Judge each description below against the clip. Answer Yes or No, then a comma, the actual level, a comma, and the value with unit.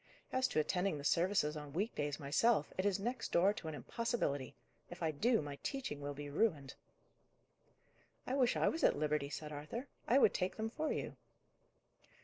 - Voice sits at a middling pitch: Yes, medium, 170 Hz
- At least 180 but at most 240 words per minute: Yes, average, 185 wpm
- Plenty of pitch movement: Yes, wide, 7.5 semitones